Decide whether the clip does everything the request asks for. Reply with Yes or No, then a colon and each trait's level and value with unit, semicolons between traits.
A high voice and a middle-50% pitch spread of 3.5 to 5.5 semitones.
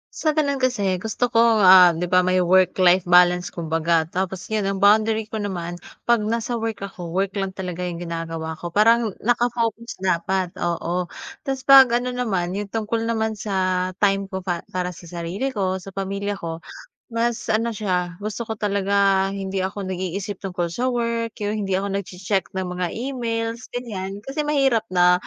Yes: high, 195 Hz; average, 3.9 semitones